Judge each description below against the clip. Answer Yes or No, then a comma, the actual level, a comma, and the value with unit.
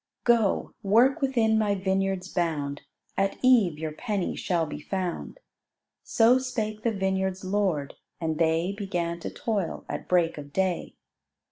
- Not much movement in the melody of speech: No, average, 4.1 semitones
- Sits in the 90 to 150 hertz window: No, high, 190 Hz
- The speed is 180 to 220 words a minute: No, average, 140 wpm